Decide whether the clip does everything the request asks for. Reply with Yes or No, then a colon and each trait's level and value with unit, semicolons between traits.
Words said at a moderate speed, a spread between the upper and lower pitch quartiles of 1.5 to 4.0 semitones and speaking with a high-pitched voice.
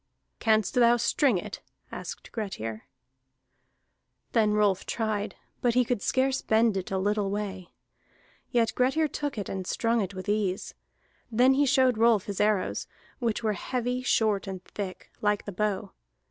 Yes: average, 155 wpm; average, 3.5 semitones; high, 215 Hz